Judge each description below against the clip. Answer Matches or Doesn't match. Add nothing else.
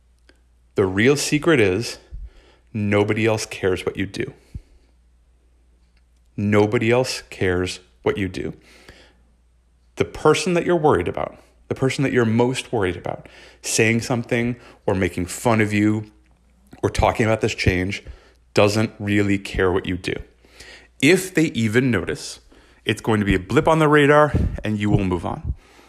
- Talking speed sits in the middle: Matches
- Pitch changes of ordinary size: Doesn't match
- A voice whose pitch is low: Matches